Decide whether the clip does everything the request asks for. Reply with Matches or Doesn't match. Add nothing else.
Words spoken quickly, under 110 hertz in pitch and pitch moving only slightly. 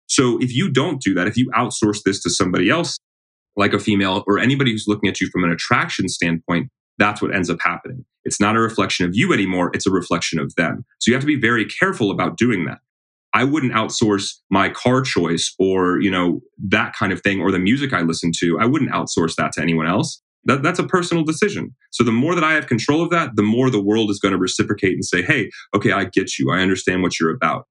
Doesn't match